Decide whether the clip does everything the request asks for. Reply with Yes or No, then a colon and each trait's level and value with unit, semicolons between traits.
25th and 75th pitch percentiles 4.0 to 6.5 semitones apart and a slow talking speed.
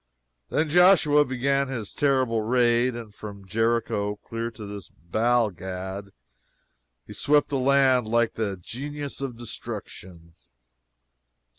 Yes: average, 4.8 semitones; slow, 120 wpm